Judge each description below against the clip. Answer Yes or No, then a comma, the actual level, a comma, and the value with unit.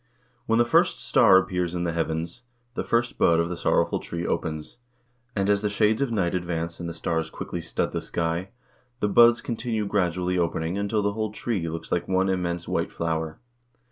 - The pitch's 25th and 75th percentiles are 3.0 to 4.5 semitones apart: Yes, average, 3.7 semitones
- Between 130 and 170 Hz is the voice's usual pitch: No, very low, 90 Hz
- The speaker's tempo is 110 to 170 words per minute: No, average, 195 wpm